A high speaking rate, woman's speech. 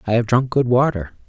No: fast, 235 wpm; male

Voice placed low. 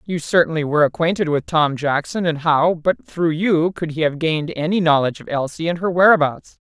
No: medium, 160 Hz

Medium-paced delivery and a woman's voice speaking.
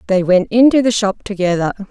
Yes: average, 190 wpm; female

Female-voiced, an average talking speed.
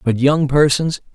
No: male; average, 155 wpm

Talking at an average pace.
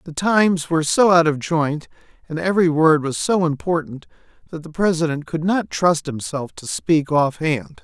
Yes: average, 185 wpm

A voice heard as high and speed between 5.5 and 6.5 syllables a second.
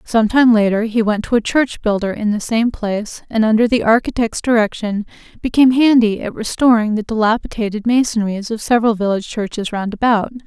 Yes: high, 220 Hz; 5.7 syllables/s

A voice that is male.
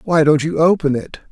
Yes: male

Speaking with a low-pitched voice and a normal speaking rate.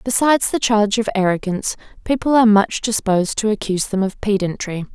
No: high, 210 Hz; average, 170 wpm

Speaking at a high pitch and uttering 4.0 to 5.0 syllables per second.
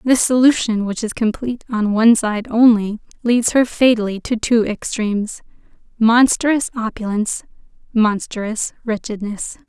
Yes: high, 225 Hz; 4.5 syllables/s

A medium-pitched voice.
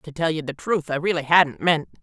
Yes: medium, 155 Hz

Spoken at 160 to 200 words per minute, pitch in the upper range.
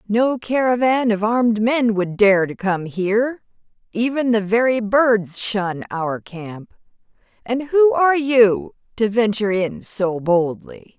No: average, 140 wpm; high, 220 Hz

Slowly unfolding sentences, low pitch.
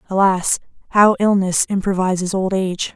No: slow, 120 wpm; high, 190 Hz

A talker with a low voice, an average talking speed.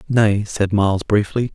Yes: low, 105 Hz; average, 155 wpm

